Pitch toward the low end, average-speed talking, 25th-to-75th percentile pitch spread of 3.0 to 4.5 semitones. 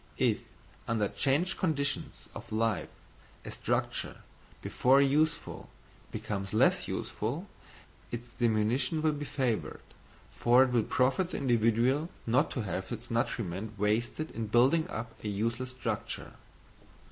No: low, 120 Hz; slow, 125 wpm; average, 4.1 semitones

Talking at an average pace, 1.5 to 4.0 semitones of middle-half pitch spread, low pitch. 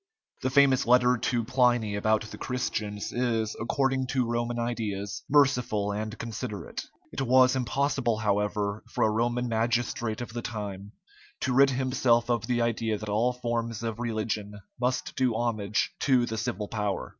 Yes: average, 155 wpm; narrow, 2.6 semitones; low, 115 Hz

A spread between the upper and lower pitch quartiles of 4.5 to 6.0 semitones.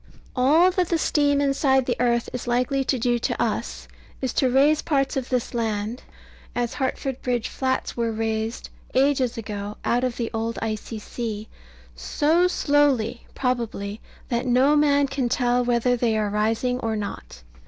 No: average, 3.2 semitones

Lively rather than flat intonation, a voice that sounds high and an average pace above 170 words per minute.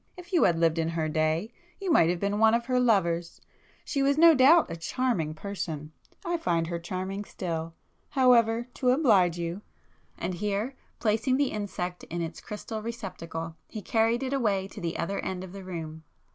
Yes: wide, 6.1 semitones; high, 195 Hz; average, 185 wpm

